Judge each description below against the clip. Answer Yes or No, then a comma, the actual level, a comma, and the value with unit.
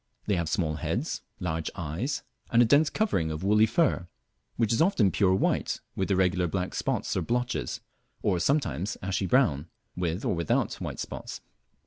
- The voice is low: Yes, very low, 95 Hz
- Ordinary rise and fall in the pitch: No, wide, 5.7 semitones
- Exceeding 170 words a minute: No, average, 165 wpm